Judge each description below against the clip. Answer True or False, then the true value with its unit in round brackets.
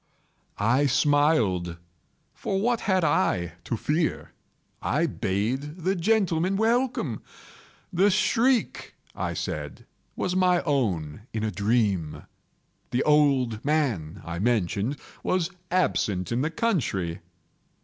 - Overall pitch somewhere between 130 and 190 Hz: True (140 Hz)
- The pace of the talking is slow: True (110 wpm)